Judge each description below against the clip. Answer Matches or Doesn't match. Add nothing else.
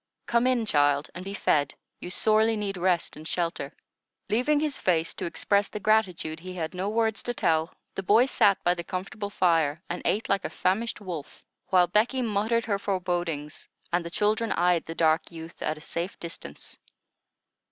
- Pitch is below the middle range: Doesn't match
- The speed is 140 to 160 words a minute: Doesn't match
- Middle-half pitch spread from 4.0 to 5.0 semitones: Matches